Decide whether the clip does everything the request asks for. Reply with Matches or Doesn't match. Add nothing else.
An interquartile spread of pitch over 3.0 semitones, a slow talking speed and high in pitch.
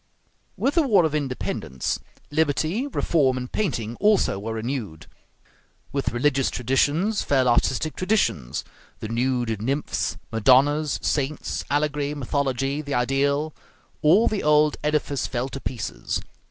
Doesn't match